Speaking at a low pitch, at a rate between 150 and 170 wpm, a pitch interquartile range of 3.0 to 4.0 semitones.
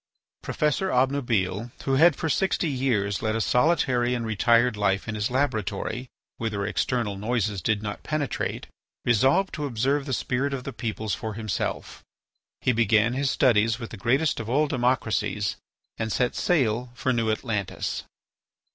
Yes: low, 120 Hz; average, 155 wpm; average, 3.6 semitones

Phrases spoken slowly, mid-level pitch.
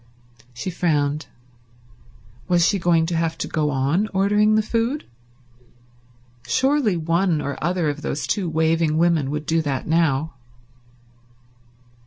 Yes: slow, 130 wpm; medium, 165 Hz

